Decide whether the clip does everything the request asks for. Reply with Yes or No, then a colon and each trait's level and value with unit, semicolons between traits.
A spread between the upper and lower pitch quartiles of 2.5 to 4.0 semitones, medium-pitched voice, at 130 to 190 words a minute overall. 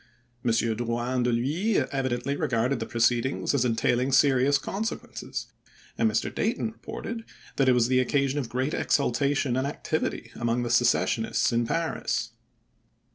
No: average, 3.0 semitones; low, 130 Hz; average, 145 wpm